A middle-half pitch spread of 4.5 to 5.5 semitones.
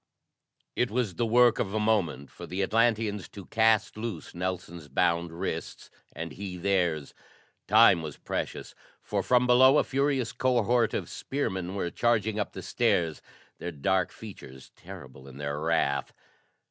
Yes: average, 5.2 semitones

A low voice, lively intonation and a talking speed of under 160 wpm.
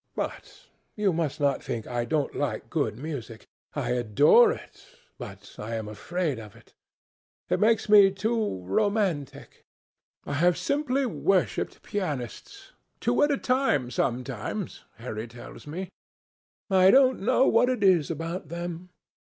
No: medium, 170 Hz; wide, 9.0 semitones; slow, 135 wpm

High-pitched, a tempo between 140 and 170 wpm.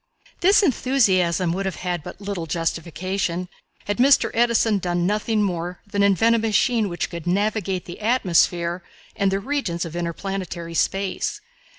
Yes: high, 195 Hz; average, 150 wpm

